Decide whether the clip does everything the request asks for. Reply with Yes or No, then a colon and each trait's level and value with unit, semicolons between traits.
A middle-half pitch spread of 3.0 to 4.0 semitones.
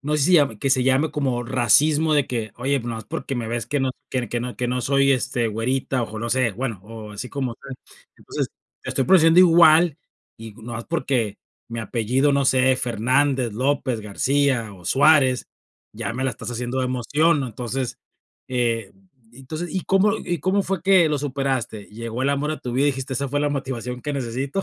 Yes: average, 3.4 semitones